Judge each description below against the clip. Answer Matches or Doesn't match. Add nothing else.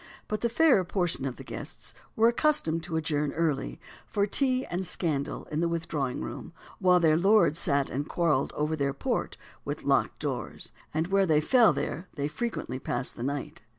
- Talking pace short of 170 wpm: Doesn't match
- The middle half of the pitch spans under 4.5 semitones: Doesn't match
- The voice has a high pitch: Doesn't match